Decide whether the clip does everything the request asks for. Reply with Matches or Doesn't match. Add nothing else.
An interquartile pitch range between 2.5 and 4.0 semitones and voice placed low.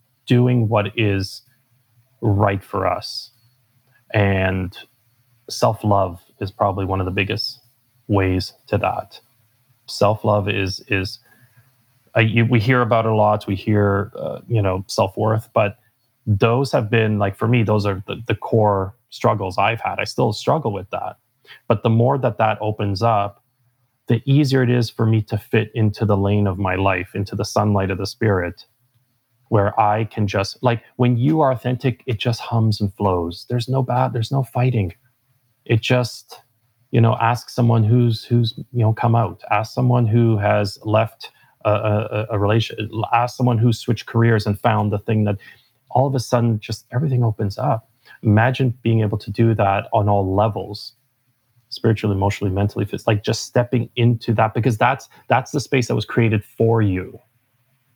Matches